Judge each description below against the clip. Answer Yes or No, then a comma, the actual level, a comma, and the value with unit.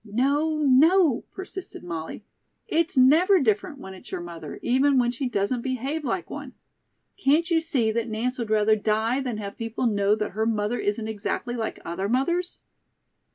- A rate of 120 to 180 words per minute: Yes, average, 170 wpm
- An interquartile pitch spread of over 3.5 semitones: Yes, average, 5.2 semitones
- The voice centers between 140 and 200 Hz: No, high, 240 Hz